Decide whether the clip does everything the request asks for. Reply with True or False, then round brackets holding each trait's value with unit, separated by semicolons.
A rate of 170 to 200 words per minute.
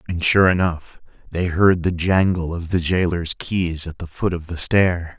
True (195 wpm)